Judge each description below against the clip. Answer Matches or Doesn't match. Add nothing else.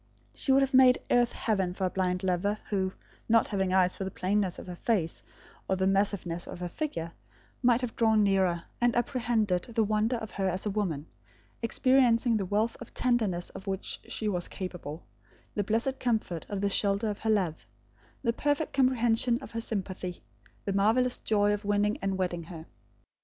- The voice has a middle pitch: Doesn't match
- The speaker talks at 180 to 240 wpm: Matches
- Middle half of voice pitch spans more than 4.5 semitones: Doesn't match